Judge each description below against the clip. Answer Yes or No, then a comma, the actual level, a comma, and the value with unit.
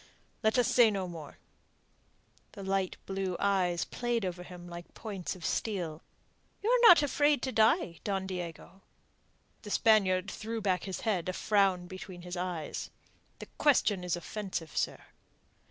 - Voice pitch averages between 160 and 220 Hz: Yes, high, 190 Hz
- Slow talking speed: No, average, 155 wpm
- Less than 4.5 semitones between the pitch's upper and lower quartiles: Yes, average, 3.5 semitones